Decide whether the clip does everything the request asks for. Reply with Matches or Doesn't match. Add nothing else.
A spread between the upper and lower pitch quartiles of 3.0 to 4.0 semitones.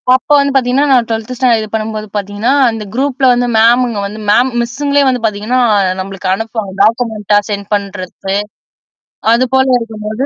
Matches